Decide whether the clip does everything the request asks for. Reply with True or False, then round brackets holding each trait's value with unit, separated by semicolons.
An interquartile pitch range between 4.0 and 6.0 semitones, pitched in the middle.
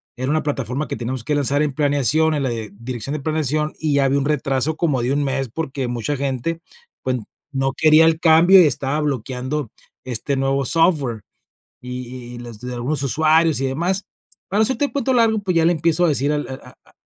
False (3.5 semitones; 145 Hz)